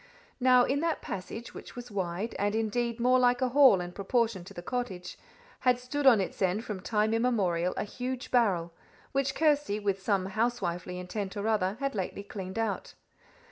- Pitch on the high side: Yes, high, 220 Hz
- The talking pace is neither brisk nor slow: Yes, average, 180 wpm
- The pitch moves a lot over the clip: No, average, 4.7 semitones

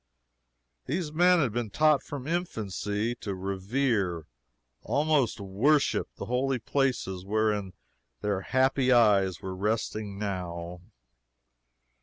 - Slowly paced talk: Yes, slow, 110 wpm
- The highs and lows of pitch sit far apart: Yes, wide, 5.7 semitones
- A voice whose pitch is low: Yes, low, 110 Hz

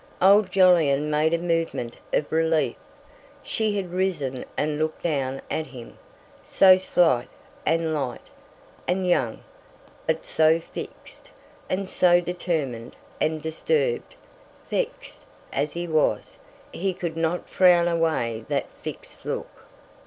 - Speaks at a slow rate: Yes, slow, 125 wpm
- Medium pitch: Yes, medium, 165 Hz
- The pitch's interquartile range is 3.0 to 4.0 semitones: Yes, average, 3.3 semitones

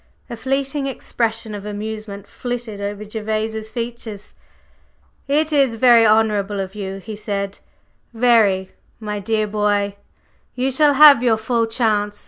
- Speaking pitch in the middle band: No, high, 220 Hz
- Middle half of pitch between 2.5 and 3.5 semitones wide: Yes, average, 2.8 semitones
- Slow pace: Yes, slow, 130 wpm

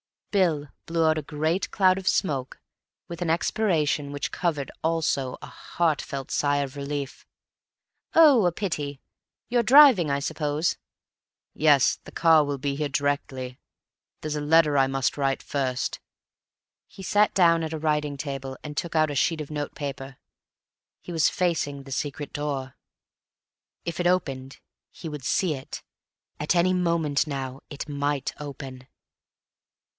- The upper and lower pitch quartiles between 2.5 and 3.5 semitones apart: Yes, average, 3.1 semitones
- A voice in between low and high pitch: Yes, medium, 150 Hz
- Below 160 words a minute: Yes, average, 150 wpm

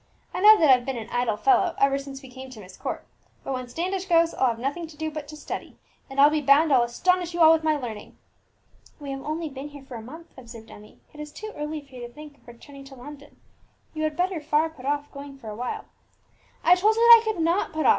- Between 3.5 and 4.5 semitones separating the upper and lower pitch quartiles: Yes, average, 3.8 semitones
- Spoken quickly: Yes, fast, 265 wpm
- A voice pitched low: No, very high, 290 Hz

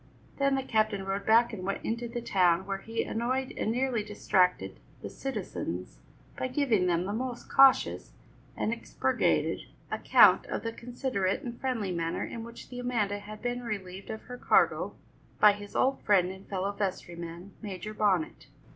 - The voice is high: Yes, high, 215 Hz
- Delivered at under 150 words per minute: No, average, 165 wpm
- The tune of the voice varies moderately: Yes, average, 4.0 semitones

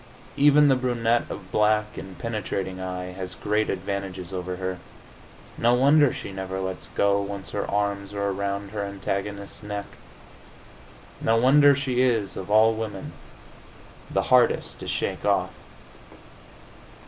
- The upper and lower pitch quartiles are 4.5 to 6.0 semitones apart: No, average, 3.0 semitones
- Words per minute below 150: Yes, slow, 135 wpm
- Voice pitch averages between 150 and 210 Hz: No, low, 100 Hz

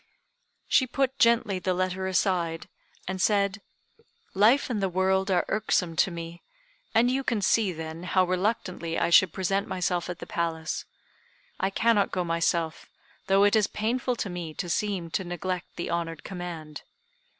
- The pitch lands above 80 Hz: Yes, medium, 185 Hz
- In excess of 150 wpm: Yes, average, 160 wpm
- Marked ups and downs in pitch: No, average, 3.1 semitones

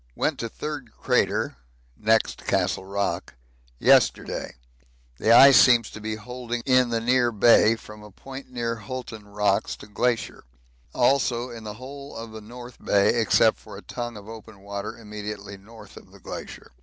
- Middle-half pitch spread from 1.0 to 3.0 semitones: Yes, average, 2.7 semitones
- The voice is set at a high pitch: No, low, 115 Hz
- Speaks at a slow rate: No, average, 165 wpm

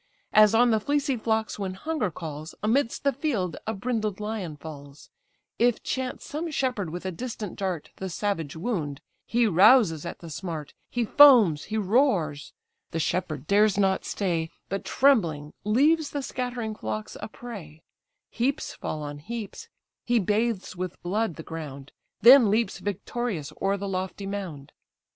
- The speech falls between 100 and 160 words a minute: Yes, average, 155 wpm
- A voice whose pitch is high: Yes, high, 200 Hz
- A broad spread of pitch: Yes, wide, 6.6 semitones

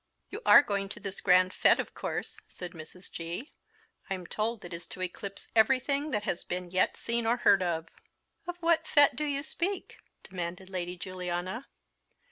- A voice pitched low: No, high, 195 Hz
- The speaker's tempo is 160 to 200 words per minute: Yes, average, 175 wpm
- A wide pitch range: Yes, wide, 5.7 semitones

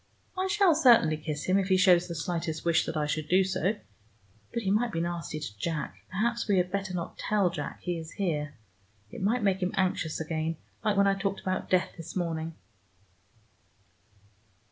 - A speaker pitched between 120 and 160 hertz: No, medium, 180 Hz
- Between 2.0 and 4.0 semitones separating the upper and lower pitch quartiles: Yes, average, 3.5 semitones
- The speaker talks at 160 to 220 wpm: Yes, average, 190 wpm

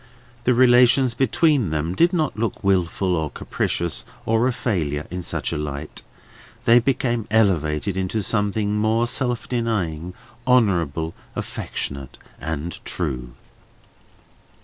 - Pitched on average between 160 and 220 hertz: No, low, 100 Hz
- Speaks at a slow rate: Yes, slow, 120 wpm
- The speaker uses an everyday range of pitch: No, wide, 6.8 semitones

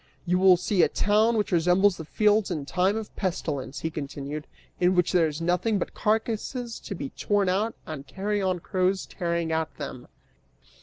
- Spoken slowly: No, average, 175 wpm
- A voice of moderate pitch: Yes, medium, 180 Hz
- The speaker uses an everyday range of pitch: Yes, average, 4.2 semitones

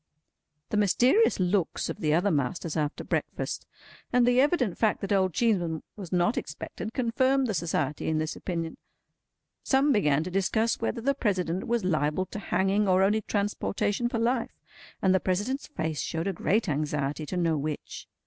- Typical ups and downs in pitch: No, wide, 5.8 semitones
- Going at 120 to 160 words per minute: No, average, 170 wpm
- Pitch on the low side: No, high, 190 Hz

